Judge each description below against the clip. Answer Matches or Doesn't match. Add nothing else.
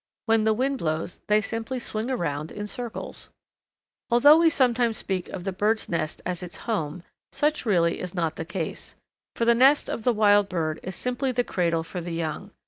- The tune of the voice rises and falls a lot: Matches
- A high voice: Matches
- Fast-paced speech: Doesn't match